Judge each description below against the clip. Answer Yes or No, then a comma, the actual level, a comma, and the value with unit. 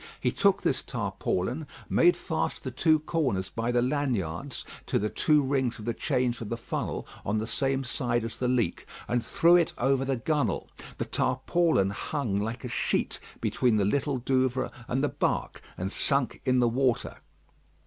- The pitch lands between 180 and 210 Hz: No, low, 125 Hz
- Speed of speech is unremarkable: Yes, average, 180 wpm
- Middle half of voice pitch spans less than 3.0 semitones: No, average, 3.5 semitones